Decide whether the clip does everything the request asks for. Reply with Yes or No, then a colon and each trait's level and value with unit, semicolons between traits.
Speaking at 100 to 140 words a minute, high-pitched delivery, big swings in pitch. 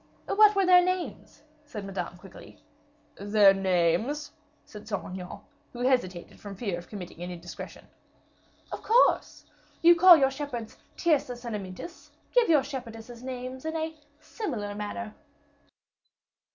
Yes: slow, 135 wpm; high, 240 Hz; wide, 7.4 semitones